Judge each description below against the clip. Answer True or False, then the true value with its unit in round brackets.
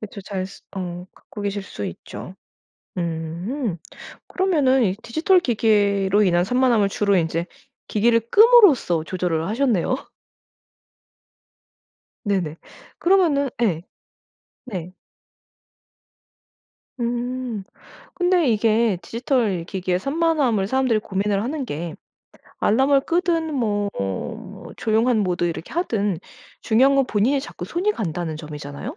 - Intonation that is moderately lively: False (6.5 semitones)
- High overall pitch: True (215 Hz)